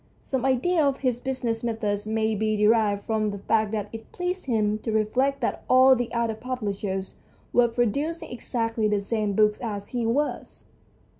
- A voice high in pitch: Yes, high, 225 Hz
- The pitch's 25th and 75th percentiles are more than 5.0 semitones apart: No, average, 3.2 semitones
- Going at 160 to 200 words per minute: Yes, average, 170 wpm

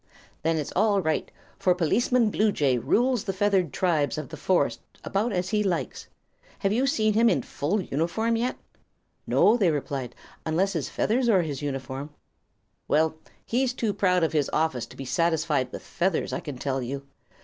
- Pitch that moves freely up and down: Yes, wide, 6.3 semitones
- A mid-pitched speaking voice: Yes, medium, 175 Hz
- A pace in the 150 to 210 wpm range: Yes, average, 175 wpm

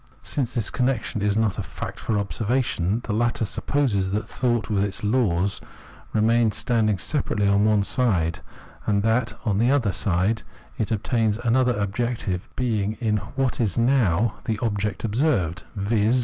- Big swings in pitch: No, average, 3.0 semitones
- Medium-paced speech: Yes, average, 155 wpm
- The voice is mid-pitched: No, low, 110 Hz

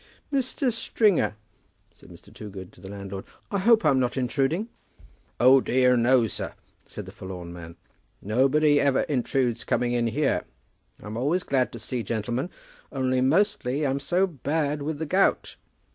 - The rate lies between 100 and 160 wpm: Yes, average, 155 wpm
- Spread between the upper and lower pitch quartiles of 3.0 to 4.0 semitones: No, average, 4.6 semitones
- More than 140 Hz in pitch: No, low, 130 Hz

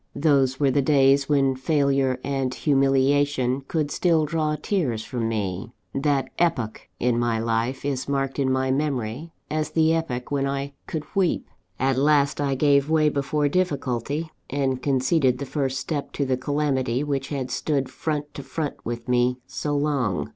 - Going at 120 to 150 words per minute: No, average, 165 wpm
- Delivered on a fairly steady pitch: Yes, narrow, 2.3 semitones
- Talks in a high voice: No, medium, 140 Hz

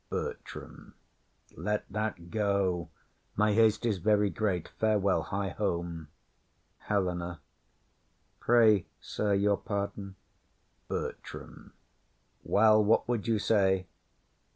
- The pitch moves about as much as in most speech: No, narrow, 2.2 semitones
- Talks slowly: Yes, slow, 95 wpm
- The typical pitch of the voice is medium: No, low, 100 Hz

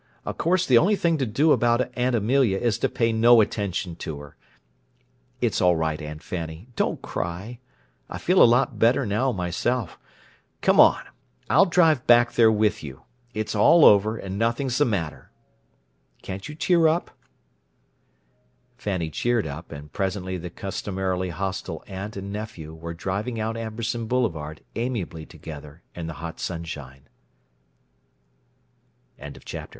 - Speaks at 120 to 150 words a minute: Yes, average, 145 wpm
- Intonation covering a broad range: Yes, wide, 6.1 semitones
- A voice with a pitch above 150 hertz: No, low, 105 Hz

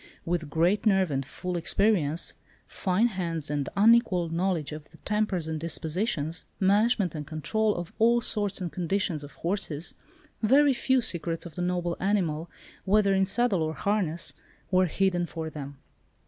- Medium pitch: Yes, medium, 180 Hz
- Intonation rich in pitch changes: No, average, 4.2 semitones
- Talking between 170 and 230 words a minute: No, average, 155 wpm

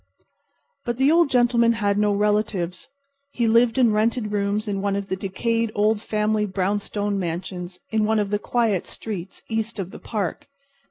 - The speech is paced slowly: No, average, 170 wpm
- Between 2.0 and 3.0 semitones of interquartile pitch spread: Yes, narrow, 2.4 semitones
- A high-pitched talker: Yes, high, 210 Hz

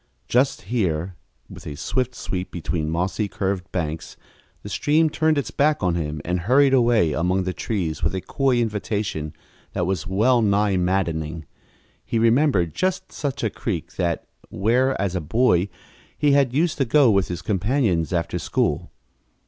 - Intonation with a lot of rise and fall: Yes, wide, 6.6 semitones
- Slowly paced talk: No, average, 165 wpm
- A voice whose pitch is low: Yes, low, 100 Hz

